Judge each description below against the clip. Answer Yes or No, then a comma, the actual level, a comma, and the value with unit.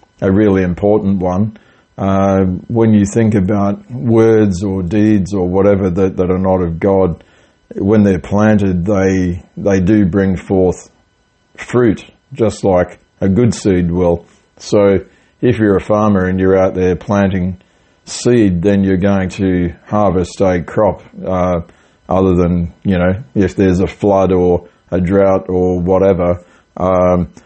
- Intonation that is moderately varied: No, narrow, 2.0 semitones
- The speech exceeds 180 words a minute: No, average, 150 wpm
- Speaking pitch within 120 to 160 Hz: No, very low, 95 Hz